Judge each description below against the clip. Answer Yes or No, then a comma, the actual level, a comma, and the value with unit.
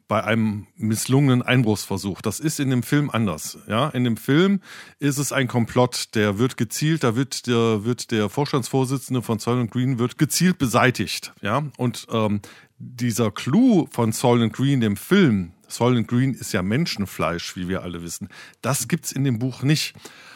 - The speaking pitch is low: Yes, low, 120 Hz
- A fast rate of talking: No, average, 175 wpm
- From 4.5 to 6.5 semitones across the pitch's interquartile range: No, average, 3.8 semitones